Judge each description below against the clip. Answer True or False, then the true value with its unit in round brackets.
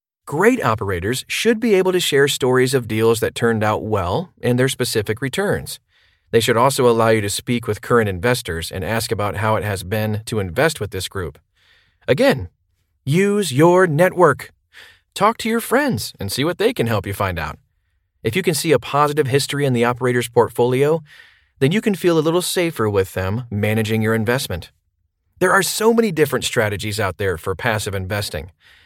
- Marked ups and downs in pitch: True (6.8 semitones)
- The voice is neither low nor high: False (120 Hz)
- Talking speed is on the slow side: False (190 wpm)